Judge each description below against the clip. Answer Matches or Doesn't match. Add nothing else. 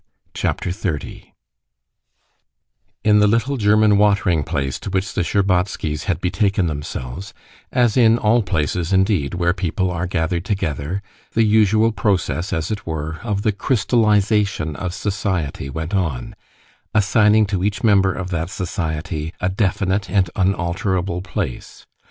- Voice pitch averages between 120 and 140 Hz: Doesn't match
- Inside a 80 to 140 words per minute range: Matches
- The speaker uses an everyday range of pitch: Matches